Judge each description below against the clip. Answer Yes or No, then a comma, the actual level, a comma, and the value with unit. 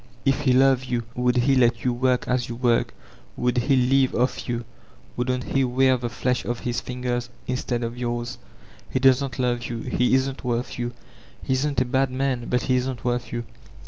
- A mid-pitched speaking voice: No, low, 125 Hz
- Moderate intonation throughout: No, narrow, 1.3 semitones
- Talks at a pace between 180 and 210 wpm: Yes, average, 200 wpm